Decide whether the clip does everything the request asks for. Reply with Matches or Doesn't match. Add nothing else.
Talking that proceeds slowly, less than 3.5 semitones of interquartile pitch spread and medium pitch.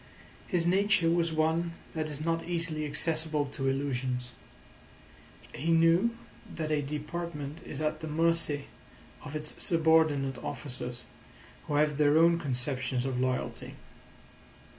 Matches